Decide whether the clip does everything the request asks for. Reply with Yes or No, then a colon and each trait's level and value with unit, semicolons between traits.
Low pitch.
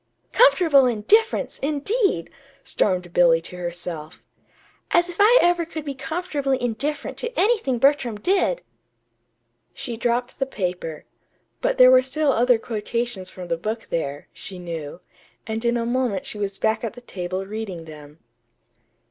No: high, 235 Hz